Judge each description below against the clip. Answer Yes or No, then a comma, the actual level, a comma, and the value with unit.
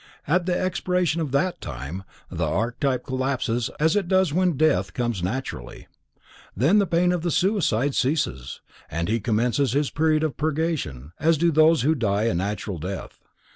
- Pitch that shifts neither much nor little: No, wide, 7.4 semitones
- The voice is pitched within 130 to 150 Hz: Yes, medium, 140 Hz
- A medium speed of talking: Yes, average, 170 wpm